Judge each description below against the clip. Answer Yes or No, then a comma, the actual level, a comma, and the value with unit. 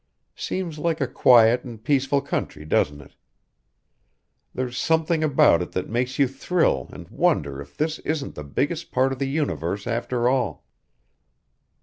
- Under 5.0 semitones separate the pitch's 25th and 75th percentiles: No, wide, 5.4 semitones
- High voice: No, low, 130 Hz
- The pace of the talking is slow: No, average, 150 wpm